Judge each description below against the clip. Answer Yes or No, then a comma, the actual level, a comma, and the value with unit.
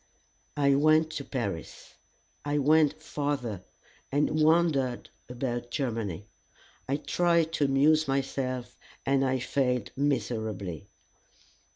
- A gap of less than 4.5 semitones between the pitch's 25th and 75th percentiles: Yes, average, 3.5 semitones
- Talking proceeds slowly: Yes, slow, 100 wpm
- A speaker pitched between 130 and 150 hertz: Yes, low, 135 Hz